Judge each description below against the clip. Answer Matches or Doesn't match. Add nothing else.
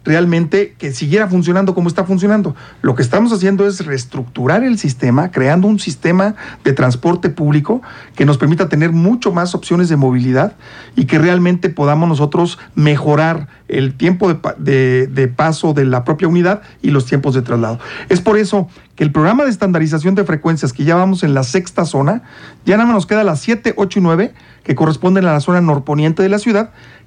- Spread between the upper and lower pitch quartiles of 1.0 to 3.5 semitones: Doesn't match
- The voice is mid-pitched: Matches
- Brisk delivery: Matches